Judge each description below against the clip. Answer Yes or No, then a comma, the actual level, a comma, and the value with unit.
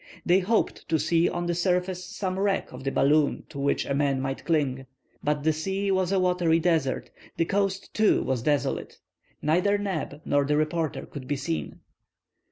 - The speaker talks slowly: No, average, 180 wpm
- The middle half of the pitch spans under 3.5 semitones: No, average, 4.5 semitones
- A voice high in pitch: No, medium, 165 Hz